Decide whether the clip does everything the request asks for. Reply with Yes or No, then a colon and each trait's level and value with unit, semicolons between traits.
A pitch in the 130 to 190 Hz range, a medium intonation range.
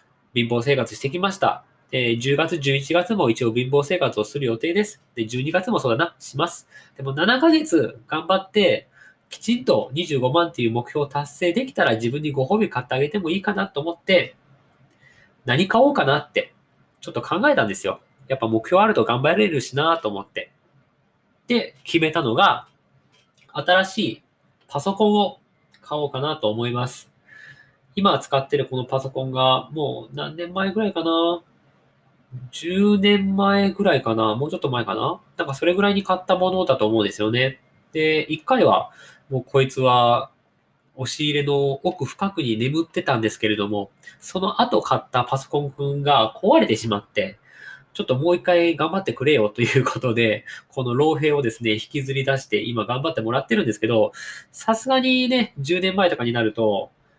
No: medium, 140 Hz; wide, 6.0 semitones